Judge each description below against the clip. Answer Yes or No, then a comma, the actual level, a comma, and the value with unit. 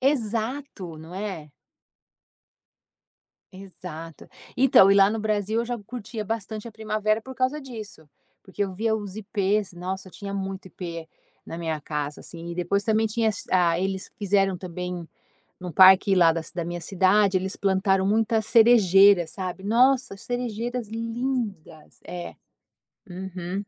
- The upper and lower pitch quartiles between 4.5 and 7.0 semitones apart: No, average, 3.5 semitones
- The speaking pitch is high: Yes, high, 195 Hz